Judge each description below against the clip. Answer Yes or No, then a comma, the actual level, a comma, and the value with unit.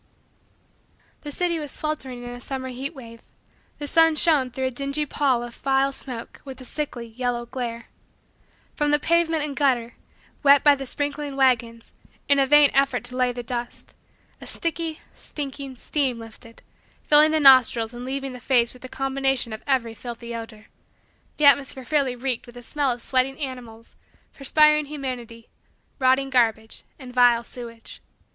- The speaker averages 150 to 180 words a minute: Yes, average, 165 wpm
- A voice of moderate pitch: No, very high, 260 Hz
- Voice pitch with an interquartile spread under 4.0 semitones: Yes, average, 2.9 semitones